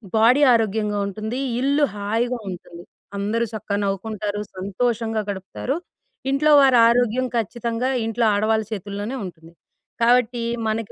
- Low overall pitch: No, high, 220 Hz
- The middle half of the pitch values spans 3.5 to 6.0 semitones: No, average, 2.9 semitones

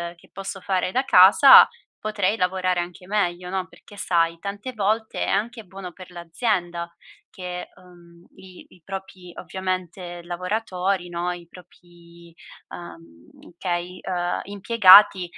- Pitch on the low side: No, medium, 180 Hz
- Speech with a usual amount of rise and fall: No, narrow, 1.9 semitones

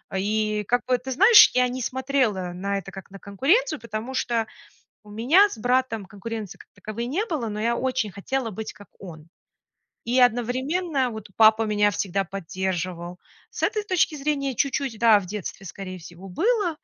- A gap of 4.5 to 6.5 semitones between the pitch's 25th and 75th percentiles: Yes, average, 4.9 semitones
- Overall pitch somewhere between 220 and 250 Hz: Yes, high, 225 Hz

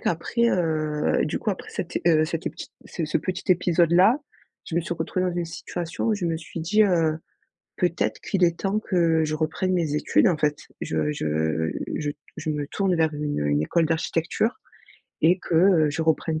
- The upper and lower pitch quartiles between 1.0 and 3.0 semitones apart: Yes, narrow, 2.6 semitones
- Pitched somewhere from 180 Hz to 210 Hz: No, medium, 165 Hz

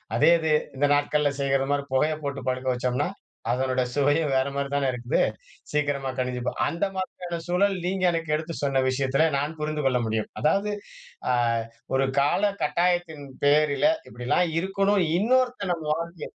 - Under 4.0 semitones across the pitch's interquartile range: No, average, 4.3 semitones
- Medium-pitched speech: Yes, medium, 150 Hz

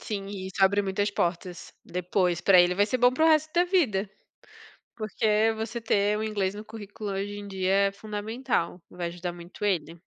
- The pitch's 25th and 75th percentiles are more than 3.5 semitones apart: No, average, 2.7 semitones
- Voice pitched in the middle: No, high, 205 Hz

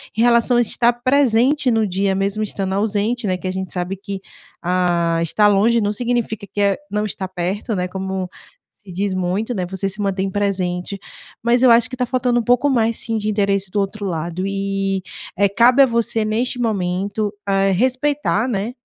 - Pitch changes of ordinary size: Yes, average, 3.5 semitones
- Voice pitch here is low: No, high, 205 Hz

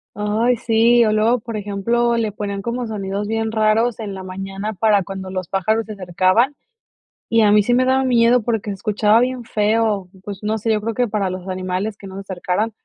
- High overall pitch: Yes, high, 215 Hz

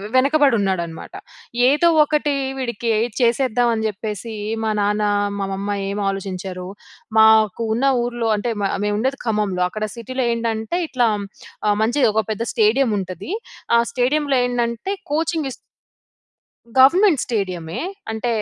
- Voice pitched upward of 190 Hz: Yes, high, 230 Hz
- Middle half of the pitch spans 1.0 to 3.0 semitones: No, average, 4.1 semitones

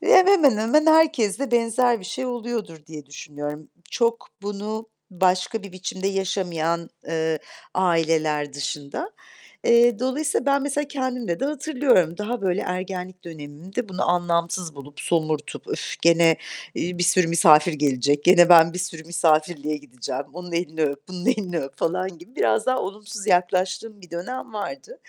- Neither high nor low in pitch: Yes, medium, 180 Hz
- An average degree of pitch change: No, wide, 6.1 semitones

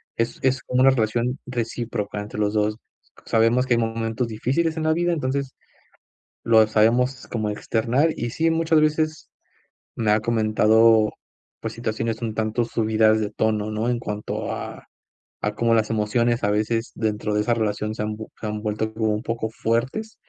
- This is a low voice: Yes, low, 115 Hz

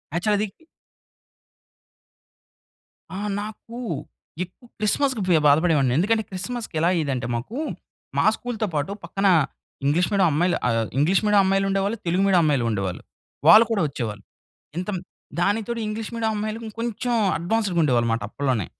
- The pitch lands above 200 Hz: No, high, 190 Hz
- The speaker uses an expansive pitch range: Yes, wide, 6.7 semitones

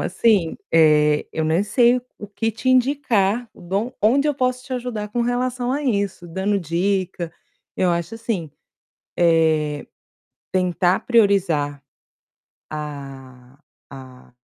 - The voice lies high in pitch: Yes, high, 195 Hz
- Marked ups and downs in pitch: Yes, wide, 6.9 semitones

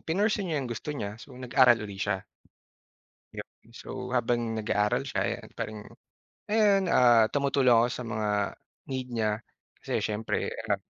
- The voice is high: No, low, 120 Hz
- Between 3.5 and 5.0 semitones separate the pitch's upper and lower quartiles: Yes, average, 4.2 semitones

